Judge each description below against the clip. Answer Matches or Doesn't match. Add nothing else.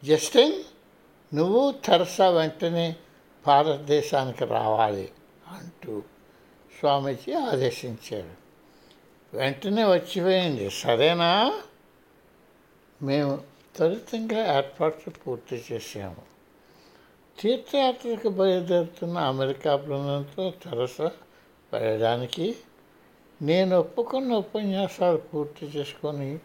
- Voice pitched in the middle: Matches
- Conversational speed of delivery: Doesn't match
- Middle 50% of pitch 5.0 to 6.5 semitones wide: Matches